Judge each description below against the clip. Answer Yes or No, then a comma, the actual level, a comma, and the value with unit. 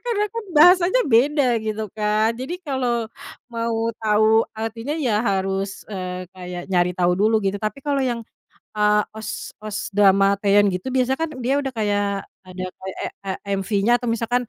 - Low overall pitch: No, high, 220 Hz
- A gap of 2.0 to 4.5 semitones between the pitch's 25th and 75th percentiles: Yes, average, 4.2 semitones